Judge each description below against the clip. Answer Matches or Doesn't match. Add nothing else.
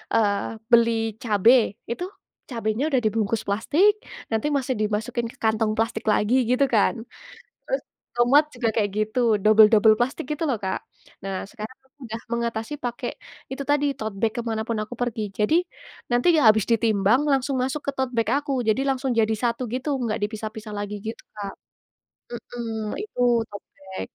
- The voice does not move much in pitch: Doesn't match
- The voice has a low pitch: Doesn't match